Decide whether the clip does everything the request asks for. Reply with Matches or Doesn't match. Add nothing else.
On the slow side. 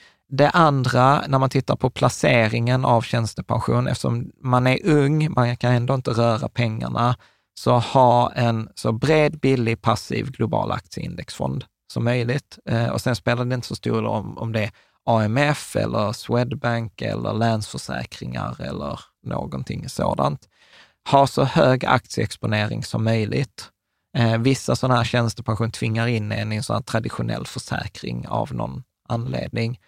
Doesn't match